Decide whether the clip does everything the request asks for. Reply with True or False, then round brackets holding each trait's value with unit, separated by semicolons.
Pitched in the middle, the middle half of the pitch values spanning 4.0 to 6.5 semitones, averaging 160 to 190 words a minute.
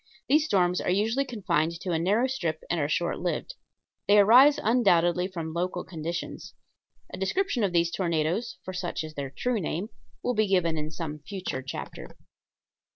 True (180 Hz; 4.3 semitones; 170 wpm)